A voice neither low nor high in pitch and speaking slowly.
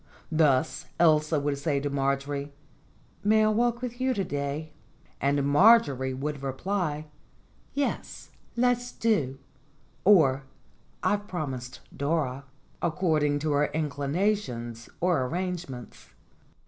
Yes: medium, 150 Hz; slow, 110 wpm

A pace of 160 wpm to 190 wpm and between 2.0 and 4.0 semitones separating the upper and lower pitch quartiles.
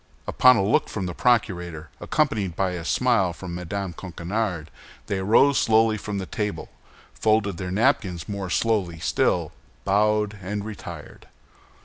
No: average, 140 wpm; average, 3.4 semitones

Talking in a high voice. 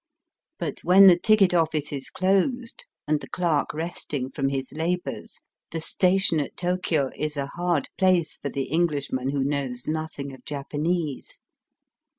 No: medium, 155 Hz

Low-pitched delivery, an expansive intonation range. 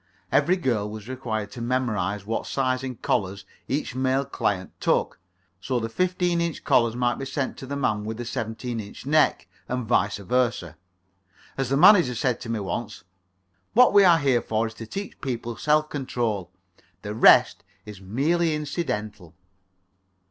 No: low, 120 Hz; average, 4.3 semitones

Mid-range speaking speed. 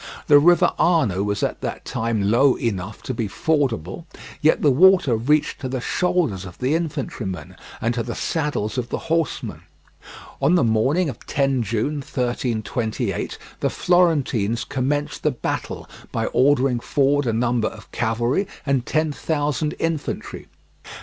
Yes: average, 150 wpm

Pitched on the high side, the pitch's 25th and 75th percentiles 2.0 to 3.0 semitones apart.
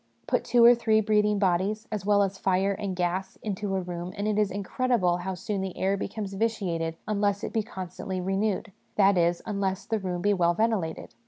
Yes: high, 195 Hz; narrow, 2.4 semitones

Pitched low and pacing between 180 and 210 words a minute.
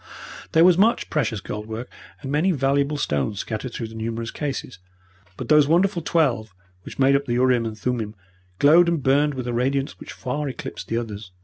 Yes: low, 130 Hz; average, 195 wpm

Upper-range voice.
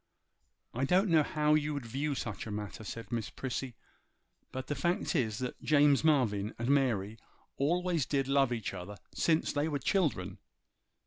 No: low, 135 Hz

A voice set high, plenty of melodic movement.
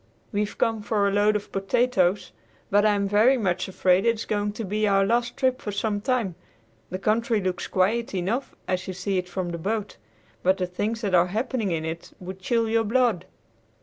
No: high, 205 Hz; average, 3.3 semitones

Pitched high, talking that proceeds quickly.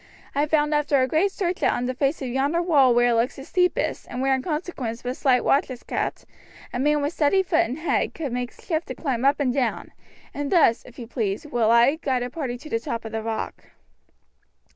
Yes: very high, 270 Hz; fast, 235 wpm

